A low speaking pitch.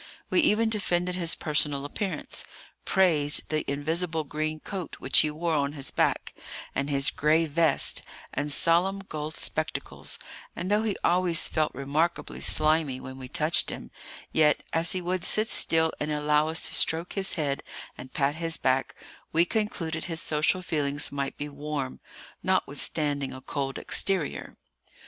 No: medium, 155 Hz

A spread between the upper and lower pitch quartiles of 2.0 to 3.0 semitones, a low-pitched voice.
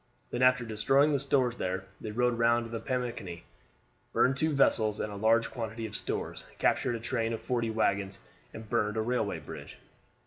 Yes: narrow, 2.4 semitones; low, 115 Hz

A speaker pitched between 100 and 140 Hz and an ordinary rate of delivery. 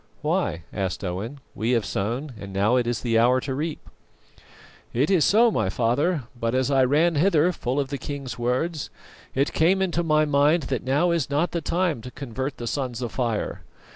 Yes: low, 135 Hz; average, 190 wpm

